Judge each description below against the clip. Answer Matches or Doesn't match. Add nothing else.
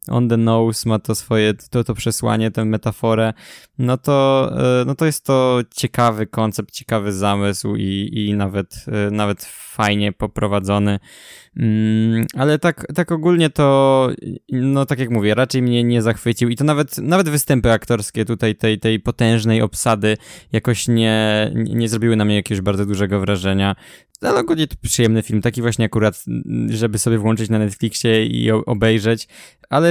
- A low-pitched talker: Matches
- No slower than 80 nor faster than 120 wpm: Doesn't match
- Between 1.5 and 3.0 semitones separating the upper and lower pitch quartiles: Matches